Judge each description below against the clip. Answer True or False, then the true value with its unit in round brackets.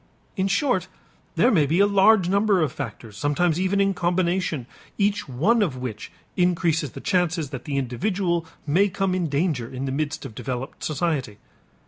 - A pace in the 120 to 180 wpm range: True (170 wpm)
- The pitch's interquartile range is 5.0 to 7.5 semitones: True (5.6 semitones)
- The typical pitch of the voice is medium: True (170 Hz)